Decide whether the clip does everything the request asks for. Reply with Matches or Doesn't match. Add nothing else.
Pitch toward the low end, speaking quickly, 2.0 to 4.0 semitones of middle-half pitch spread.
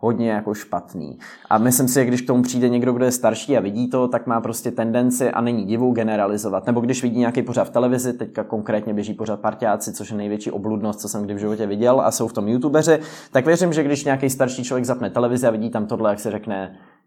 Matches